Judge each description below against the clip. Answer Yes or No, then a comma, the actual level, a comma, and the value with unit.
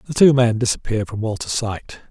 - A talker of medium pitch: No, low, 115 Hz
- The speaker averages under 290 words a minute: Yes, average, 200 wpm